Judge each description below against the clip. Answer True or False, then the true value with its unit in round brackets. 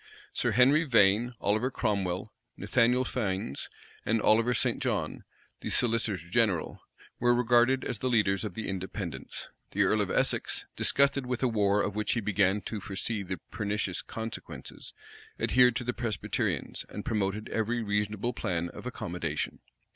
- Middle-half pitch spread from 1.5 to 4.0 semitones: True (3.6 semitones)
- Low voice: True (110 Hz)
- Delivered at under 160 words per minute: True (150 wpm)